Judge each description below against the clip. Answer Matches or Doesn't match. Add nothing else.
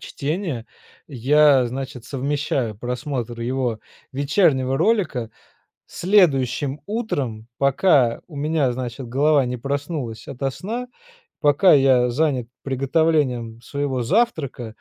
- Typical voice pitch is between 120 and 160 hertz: Matches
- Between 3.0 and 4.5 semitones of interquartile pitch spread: Matches